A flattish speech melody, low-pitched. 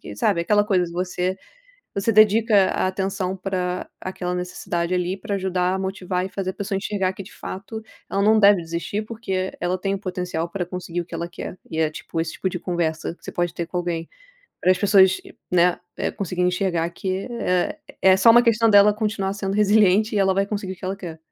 No: narrow, 1.9 semitones; high, 190 Hz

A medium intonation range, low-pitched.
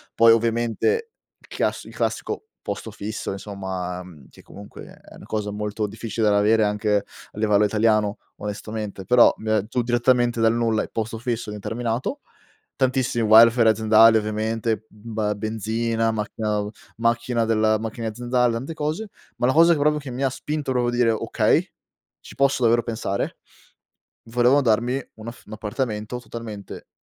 No: narrow, 2.2 semitones; low, 115 Hz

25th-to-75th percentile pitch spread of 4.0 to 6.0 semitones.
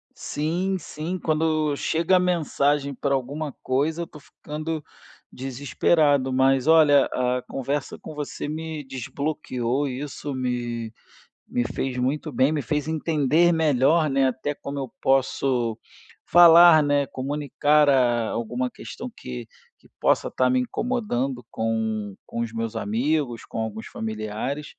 No: average, 3.6 semitones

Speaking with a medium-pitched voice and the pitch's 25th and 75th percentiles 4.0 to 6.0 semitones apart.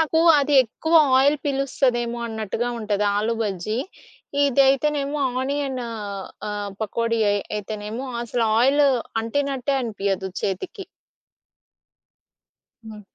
No: high, 235 Hz; average, 4.6 semitones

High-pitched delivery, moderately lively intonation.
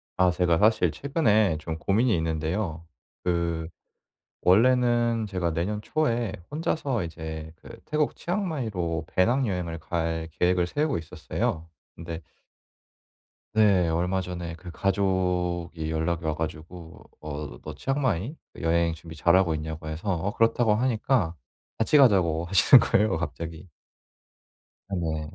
No: very low, 90 Hz; average, 4.9 semitones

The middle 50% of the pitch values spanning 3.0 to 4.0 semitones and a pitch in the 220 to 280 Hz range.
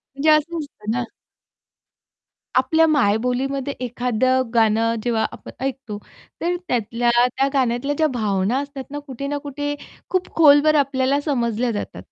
Yes: average, 3.6 semitones; very high, 260 Hz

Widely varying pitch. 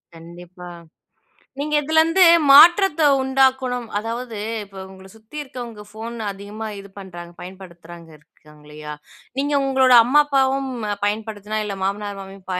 Yes: wide, 5.8 semitones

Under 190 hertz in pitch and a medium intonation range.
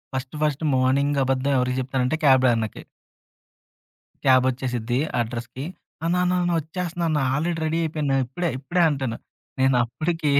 Yes: low, 135 Hz; average, 3.6 semitones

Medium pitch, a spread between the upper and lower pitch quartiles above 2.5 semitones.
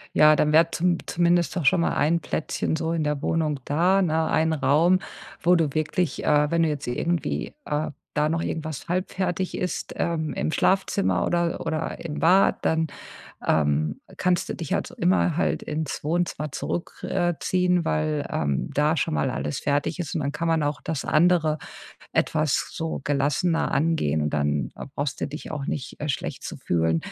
Yes: medium, 155 Hz; average, 2.9 semitones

